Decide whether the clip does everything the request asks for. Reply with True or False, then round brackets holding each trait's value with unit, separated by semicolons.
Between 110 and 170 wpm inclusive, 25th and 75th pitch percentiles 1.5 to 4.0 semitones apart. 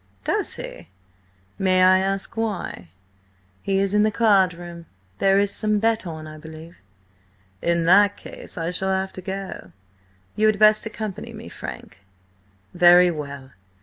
True (150 wpm; 3.2 semitones)